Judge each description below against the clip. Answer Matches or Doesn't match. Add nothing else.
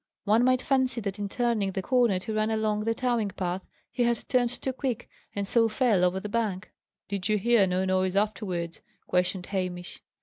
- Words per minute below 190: Doesn't match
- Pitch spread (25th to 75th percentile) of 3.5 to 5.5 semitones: Matches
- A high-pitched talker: Matches